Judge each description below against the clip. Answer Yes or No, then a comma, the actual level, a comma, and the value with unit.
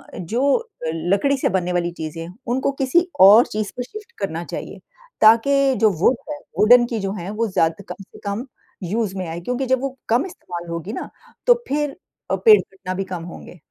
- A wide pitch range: Yes, wide, 6.5 semitones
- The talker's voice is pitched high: Yes, high, 210 Hz